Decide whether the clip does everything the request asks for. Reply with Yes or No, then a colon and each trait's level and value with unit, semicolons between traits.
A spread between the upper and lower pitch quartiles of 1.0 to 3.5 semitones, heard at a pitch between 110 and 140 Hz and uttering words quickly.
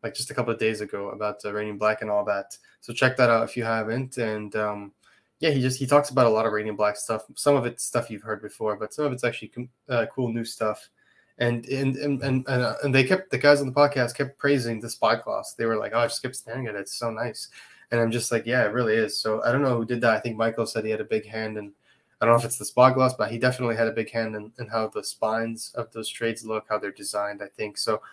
Yes: average, 2.8 semitones; low, 115 Hz; fast, 295 wpm